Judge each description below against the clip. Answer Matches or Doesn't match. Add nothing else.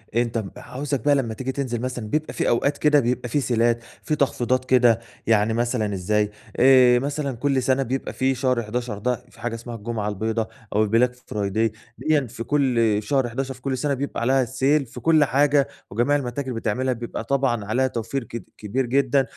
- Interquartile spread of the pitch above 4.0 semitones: Doesn't match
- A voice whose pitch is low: Matches